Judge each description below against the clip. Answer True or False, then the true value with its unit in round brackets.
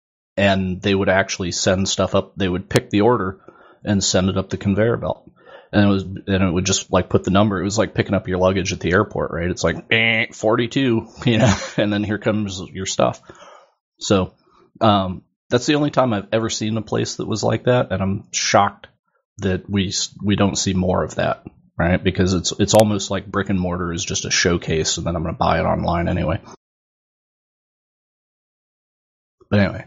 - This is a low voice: True (100 Hz)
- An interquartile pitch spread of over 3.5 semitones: False (2.6 semitones)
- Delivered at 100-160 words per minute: False (205 wpm)